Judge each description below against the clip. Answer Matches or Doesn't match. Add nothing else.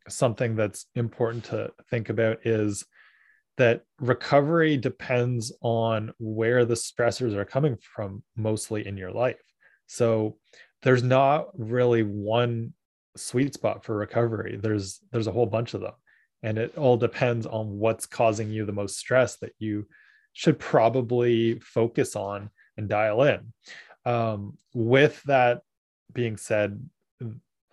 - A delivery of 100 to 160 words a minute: Matches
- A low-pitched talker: Matches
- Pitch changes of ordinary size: Doesn't match